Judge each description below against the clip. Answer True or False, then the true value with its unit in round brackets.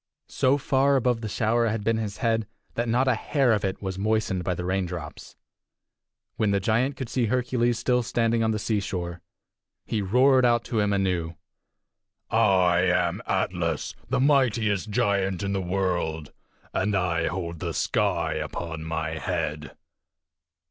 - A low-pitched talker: True (105 Hz)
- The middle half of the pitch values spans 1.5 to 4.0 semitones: False (4.4 semitones)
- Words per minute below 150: False (155 wpm)